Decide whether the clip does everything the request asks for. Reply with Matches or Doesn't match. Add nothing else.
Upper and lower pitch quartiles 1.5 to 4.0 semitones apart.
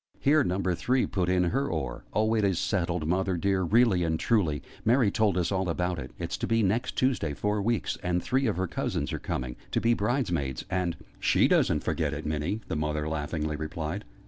Doesn't match